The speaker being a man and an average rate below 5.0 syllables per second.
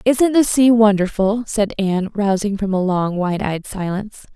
No: female; 4.7 syllables/s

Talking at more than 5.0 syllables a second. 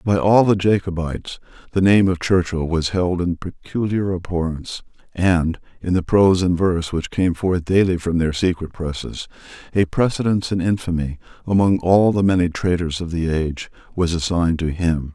Yes: 5.2 syllables/s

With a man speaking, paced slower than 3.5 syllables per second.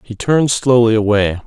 No: male; 5.2 syllables/s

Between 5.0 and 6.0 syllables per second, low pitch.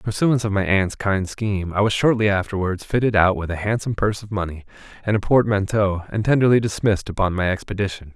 No: 6.4 syllables/s; low, 100 Hz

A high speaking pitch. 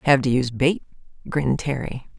No: low, 135 Hz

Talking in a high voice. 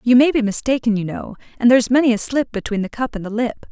Yes: high, 235 Hz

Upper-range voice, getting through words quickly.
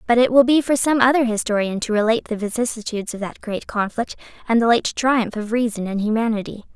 Yes: high, 225 Hz; fast, 215 wpm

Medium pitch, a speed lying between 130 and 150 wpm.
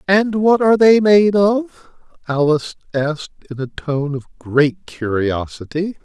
Yes: medium, 170 Hz; average, 140 wpm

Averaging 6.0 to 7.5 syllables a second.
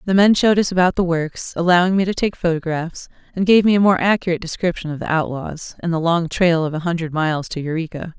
Yes: 6.2 syllables/s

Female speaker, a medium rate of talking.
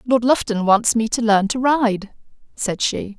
Yes: female; average, 190 wpm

